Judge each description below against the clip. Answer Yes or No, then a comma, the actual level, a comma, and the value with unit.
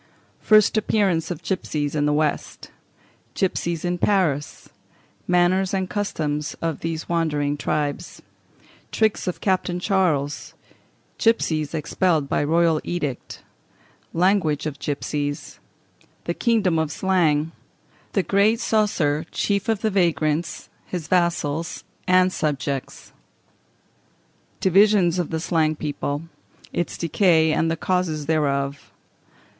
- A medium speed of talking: No, slow, 110 wpm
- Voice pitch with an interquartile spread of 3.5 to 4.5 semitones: Yes, average, 3.8 semitones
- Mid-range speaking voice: Yes, medium, 165 Hz